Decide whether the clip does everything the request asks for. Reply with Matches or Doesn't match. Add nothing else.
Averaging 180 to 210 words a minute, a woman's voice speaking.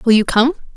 Doesn't match